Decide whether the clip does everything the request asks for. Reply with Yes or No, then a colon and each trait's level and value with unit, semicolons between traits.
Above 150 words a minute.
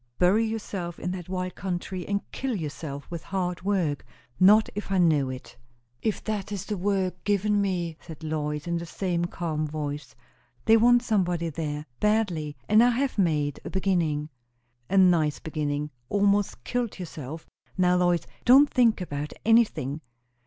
Yes: average, 160 wpm